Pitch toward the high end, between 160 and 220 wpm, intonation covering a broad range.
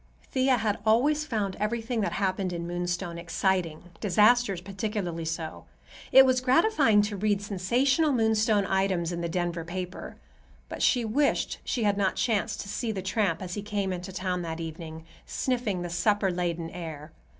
No: high, 195 Hz; average, 165 wpm; average, 4.0 semitones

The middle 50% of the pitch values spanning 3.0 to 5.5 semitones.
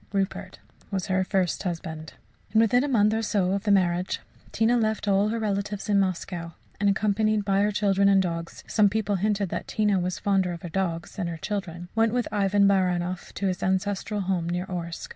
No: narrow, 2.4 semitones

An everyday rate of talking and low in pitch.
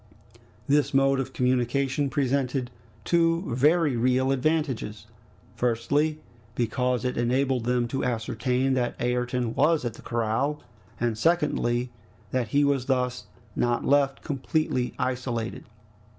No: slow, 120 wpm; low, 130 Hz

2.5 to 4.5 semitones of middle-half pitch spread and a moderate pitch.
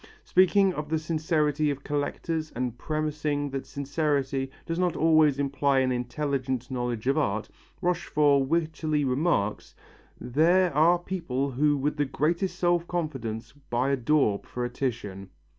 Yes: average, 3.2 semitones; medium, 145 Hz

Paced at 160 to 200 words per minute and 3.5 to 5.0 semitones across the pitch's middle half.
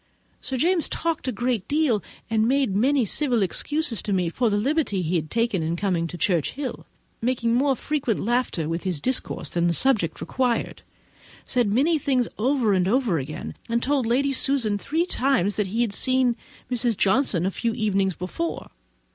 No: average, 170 wpm; wide, 5.6 semitones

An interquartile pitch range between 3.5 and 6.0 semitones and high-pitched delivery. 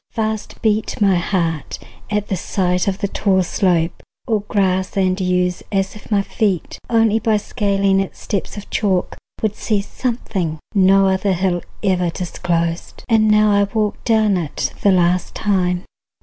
No: narrow, 2.6 semitones; high, 195 Hz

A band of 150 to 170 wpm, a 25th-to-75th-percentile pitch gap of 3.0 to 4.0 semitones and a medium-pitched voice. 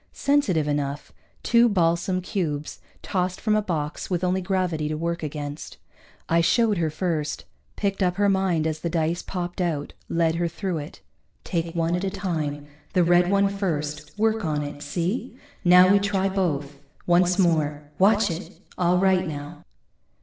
Yes: average, 165 wpm; average, 3.6 semitones; medium, 175 Hz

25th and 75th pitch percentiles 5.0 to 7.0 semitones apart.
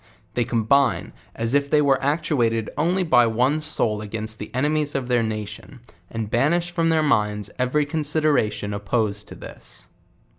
Yes: average, 5.3 semitones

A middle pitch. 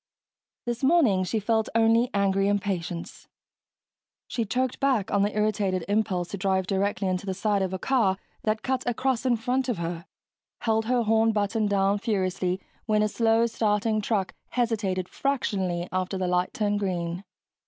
No: high, 205 Hz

